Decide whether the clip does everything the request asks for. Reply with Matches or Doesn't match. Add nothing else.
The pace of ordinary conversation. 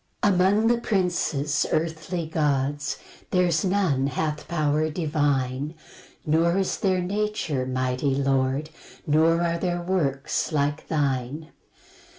Doesn't match